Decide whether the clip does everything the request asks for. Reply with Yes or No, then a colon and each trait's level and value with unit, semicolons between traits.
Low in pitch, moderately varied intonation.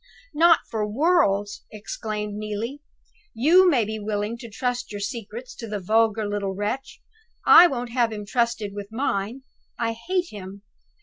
No: high, 220 Hz; average, 3.2 semitones